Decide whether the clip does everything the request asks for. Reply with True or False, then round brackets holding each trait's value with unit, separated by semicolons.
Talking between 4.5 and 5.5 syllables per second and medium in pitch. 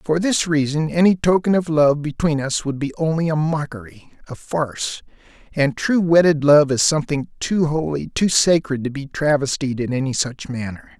True (5.0 syllables/s; 150 Hz)